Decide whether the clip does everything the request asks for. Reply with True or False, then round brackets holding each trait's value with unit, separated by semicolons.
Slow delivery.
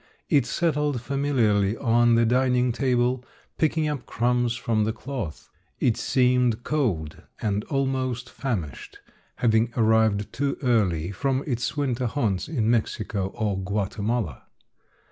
True (125 wpm)